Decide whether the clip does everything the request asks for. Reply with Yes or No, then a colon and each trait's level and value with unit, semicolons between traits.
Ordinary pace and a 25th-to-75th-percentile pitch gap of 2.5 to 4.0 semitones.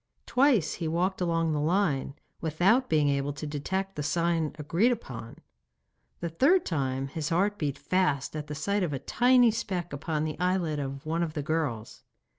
No: average, 180 wpm; average, 4.4 semitones